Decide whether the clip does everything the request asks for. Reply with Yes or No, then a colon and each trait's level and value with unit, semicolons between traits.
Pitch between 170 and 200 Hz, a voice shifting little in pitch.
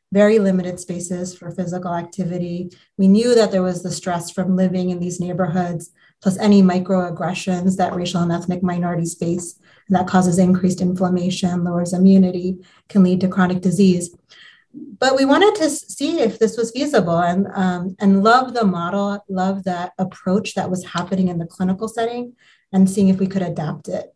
Yes: medium, 185 Hz; narrow, 1.8 semitones